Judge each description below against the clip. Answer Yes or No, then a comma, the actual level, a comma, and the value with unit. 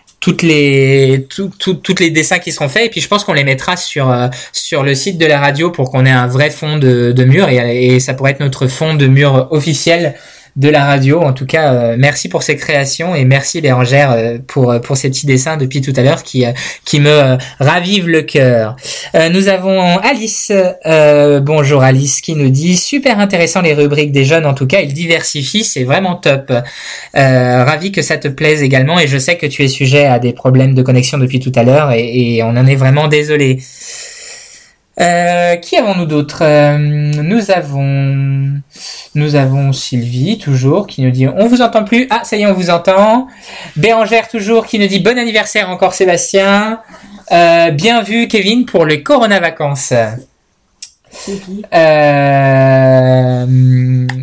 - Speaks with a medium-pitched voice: Yes, medium, 150 Hz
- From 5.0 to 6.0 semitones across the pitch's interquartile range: Yes, wide, 5.4 semitones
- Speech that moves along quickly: No, average, 190 wpm